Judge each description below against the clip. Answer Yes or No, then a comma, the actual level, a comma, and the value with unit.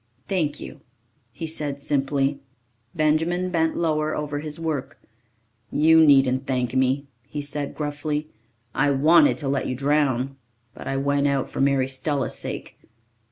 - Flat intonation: Yes, narrow, 2.2 semitones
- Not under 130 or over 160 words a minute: Yes, average, 145 wpm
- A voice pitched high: No, medium, 145 Hz